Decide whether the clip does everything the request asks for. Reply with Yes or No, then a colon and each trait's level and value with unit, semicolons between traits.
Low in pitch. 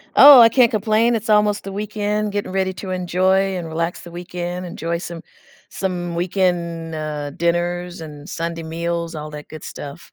No: medium, 175 Hz